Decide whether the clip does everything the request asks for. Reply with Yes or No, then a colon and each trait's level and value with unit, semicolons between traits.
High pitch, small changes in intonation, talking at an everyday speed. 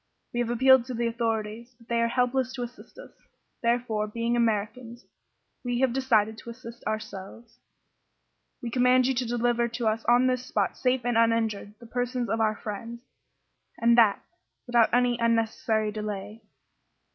Yes: high, 235 Hz; narrow, 1.8 semitones; average, 160 wpm